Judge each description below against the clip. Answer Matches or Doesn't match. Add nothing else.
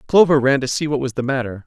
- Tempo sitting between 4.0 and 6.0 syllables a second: Doesn't match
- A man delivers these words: Matches